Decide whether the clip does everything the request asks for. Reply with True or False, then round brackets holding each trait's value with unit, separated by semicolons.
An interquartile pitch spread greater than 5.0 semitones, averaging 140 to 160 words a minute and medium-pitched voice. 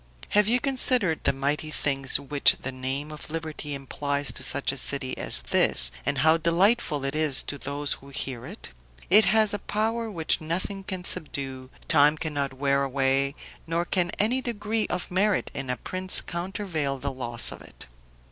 False (5.4 semitones; 175 wpm; 150 Hz)